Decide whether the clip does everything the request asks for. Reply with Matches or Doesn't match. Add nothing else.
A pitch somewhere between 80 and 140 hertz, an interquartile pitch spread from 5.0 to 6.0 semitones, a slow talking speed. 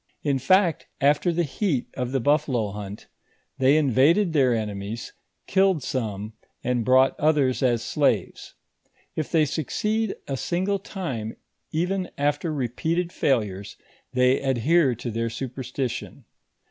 Matches